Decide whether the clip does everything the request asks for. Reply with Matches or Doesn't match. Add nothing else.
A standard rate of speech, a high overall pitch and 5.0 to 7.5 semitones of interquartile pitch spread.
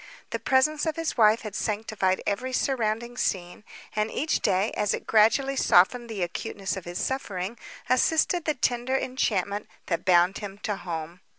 Matches